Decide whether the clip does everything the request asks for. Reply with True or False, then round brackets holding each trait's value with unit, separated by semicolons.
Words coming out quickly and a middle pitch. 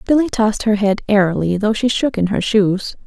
False (215 wpm; 210 Hz)